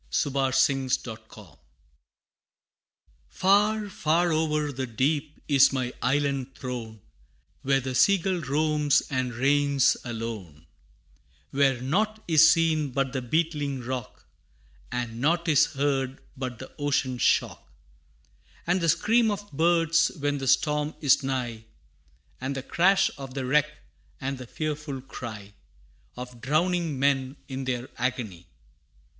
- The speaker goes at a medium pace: No, slow, 130 wpm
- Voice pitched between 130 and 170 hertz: Yes, low, 135 Hz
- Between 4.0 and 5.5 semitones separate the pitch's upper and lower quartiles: No, average, 3.4 semitones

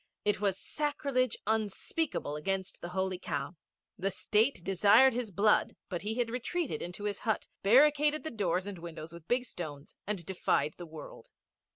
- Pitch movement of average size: No, wide, 5.7 semitones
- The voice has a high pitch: Yes, high, 200 Hz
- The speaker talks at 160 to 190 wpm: Yes, average, 165 wpm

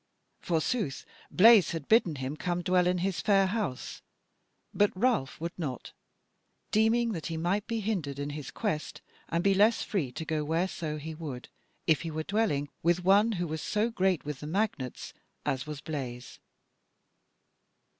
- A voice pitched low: No, medium, 170 Hz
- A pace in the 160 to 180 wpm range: Yes, average, 165 wpm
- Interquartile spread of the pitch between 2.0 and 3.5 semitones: No, average, 5.1 semitones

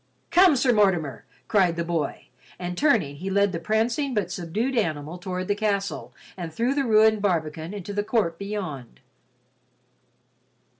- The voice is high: Yes, high, 195 Hz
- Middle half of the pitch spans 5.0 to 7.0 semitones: No, average, 4.4 semitones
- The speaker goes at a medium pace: Yes, average, 150 wpm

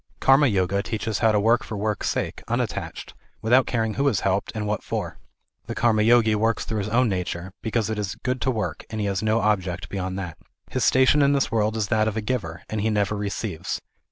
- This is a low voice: Yes, low, 110 Hz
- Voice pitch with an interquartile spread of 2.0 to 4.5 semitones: Yes, narrow, 2.4 semitones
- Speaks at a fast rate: Yes, fast, 220 wpm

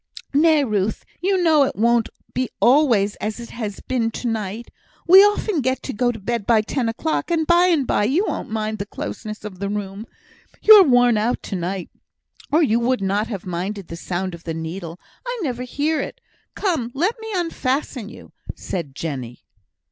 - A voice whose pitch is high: Yes, high, 235 Hz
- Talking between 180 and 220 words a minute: Yes, average, 185 wpm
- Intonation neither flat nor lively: No, wide, 6.7 semitones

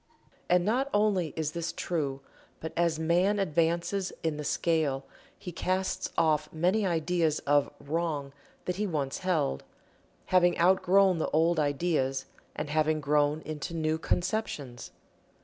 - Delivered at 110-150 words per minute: Yes, slow, 135 wpm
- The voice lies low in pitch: No, medium, 165 Hz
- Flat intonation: No, average, 3.1 semitones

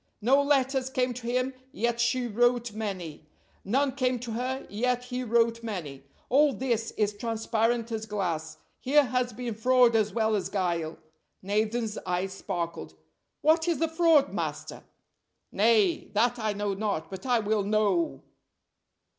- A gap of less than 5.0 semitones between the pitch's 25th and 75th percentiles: Yes, average, 3.5 semitones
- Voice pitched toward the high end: Yes, high, 230 Hz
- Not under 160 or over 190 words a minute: No, average, 150 wpm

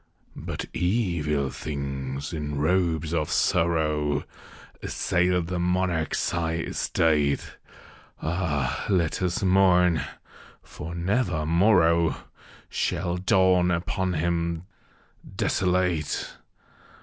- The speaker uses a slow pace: Yes, slow, 85 wpm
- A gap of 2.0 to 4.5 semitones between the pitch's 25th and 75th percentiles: Yes, average, 2.7 semitones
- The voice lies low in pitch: Yes, very low, 85 Hz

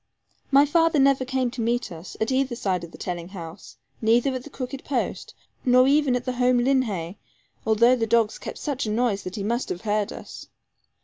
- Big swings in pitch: No, average, 3.9 semitones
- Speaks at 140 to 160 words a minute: No, average, 200 wpm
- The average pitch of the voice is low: No, high, 240 Hz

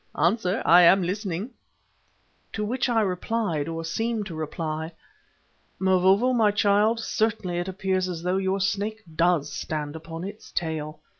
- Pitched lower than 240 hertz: Yes, medium, 185 Hz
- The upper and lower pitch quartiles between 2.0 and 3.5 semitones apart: No, average, 4.1 semitones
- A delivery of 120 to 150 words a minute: Yes, average, 145 wpm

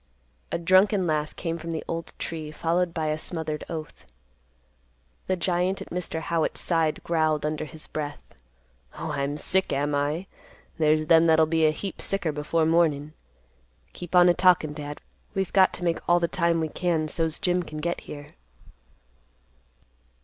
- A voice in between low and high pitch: Yes, medium, 165 Hz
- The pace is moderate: Yes, average, 165 wpm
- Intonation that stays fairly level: Yes, narrow, 2.1 semitones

